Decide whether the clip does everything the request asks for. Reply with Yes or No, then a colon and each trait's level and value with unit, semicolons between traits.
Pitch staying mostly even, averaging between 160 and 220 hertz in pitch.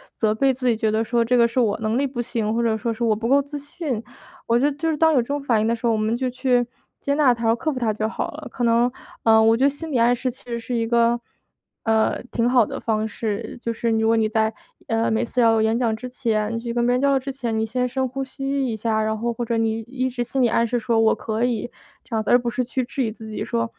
No: narrow, 2.2 semitones; high, 235 Hz